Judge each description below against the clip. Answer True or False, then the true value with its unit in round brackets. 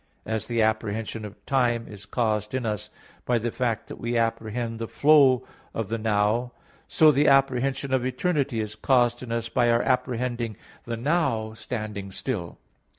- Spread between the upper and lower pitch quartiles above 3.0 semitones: False (2.6 semitones)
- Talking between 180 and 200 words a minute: False (165 wpm)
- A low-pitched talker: True (115 Hz)